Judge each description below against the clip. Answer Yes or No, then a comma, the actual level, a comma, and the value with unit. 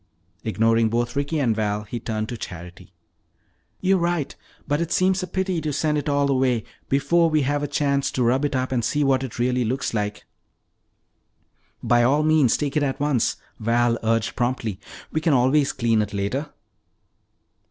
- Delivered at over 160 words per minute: Yes, average, 185 wpm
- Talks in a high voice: No, low, 130 Hz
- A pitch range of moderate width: Yes, average, 4.2 semitones